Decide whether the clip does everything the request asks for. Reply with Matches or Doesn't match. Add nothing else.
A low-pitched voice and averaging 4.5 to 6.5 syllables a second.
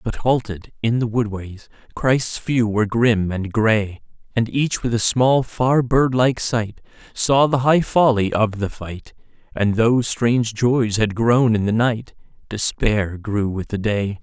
Doesn't match